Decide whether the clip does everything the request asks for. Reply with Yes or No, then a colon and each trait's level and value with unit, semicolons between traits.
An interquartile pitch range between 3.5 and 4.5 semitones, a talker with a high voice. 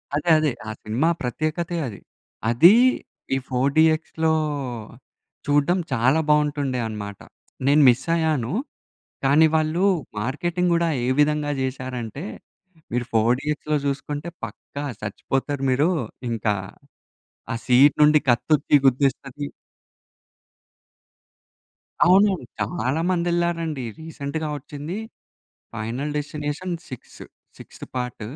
No: average, 3.9 semitones; medium, 145 Hz